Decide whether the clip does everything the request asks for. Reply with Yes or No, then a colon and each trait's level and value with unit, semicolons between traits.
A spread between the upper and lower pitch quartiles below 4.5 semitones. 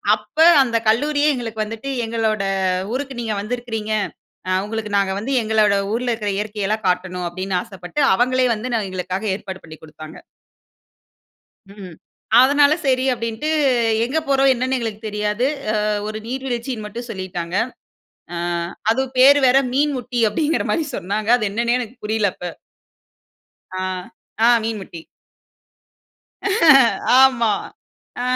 Yes: average, 3.9 semitones